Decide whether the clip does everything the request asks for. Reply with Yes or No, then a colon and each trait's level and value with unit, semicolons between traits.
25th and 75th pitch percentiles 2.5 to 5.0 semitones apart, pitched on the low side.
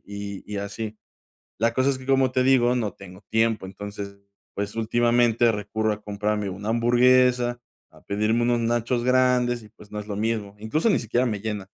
Yes: average, 2.9 semitones; low, 115 Hz